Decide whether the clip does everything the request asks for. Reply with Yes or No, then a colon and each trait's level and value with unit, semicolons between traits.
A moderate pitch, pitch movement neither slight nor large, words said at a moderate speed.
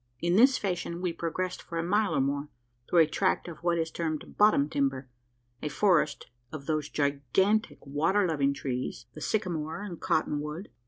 Yes: medium, 165 Hz; average, 4.0 semitones; average, 175 wpm